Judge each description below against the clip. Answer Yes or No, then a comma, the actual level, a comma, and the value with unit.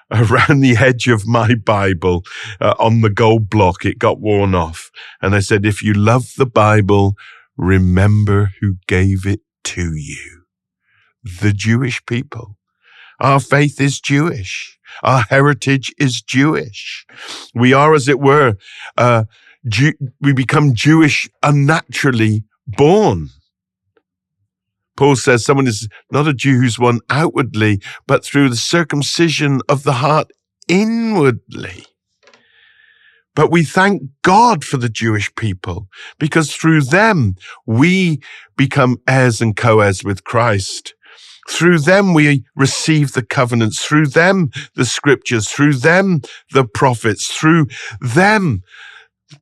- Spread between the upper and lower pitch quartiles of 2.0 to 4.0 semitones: No, wide, 5.4 semitones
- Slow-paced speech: Yes, slow, 125 wpm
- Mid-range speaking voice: No, low, 125 Hz